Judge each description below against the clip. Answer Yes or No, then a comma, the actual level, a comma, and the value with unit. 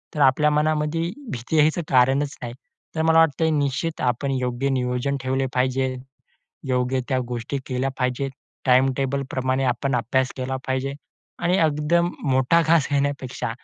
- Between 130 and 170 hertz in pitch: Yes, low, 135 Hz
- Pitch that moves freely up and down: No, average, 2.7 semitones